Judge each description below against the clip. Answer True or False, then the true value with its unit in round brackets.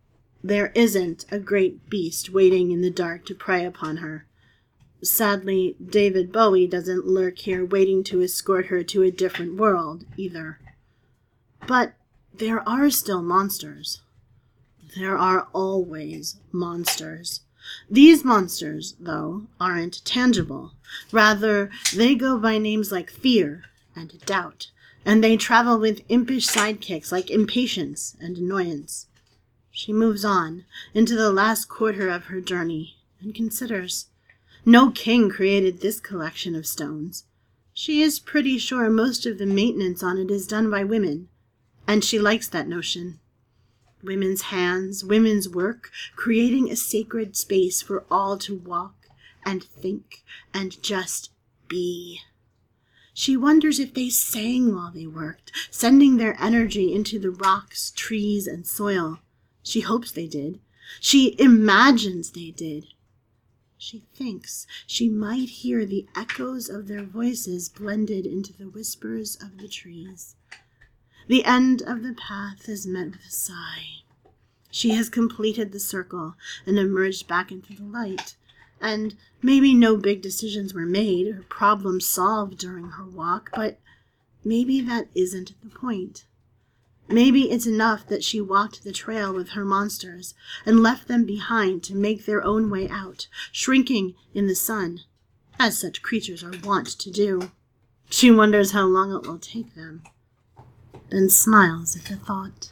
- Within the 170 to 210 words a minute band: False (140 wpm)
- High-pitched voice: True (195 Hz)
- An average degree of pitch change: True (4.1 semitones)